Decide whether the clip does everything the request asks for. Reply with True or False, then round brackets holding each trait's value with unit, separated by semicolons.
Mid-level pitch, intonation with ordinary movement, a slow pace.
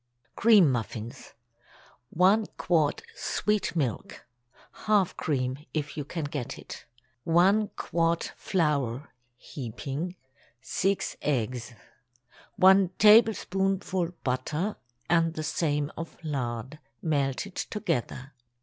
False (155 Hz; 6.0 semitones; 90 wpm)